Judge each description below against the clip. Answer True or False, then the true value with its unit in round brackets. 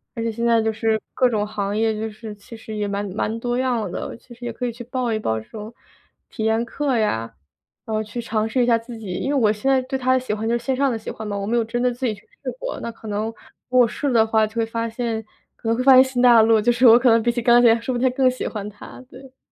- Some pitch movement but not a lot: False (2.2 semitones)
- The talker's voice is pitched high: True (230 Hz)